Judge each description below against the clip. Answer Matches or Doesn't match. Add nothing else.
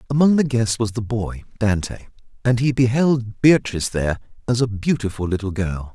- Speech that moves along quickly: Doesn't match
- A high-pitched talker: Doesn't match